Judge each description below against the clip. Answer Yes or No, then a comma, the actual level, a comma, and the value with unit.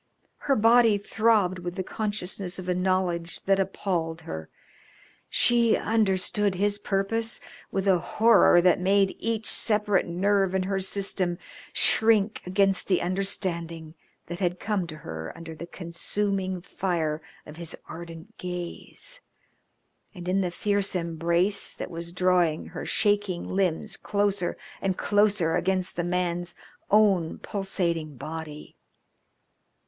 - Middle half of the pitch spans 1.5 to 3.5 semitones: Yes, average, 2.9 semitones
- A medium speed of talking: No, slow, 130 wpm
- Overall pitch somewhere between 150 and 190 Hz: Yes, medium, 185 Hz